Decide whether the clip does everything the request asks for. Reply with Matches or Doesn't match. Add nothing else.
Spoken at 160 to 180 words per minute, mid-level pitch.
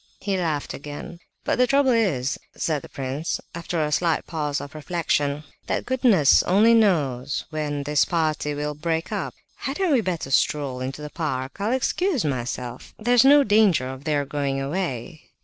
Matches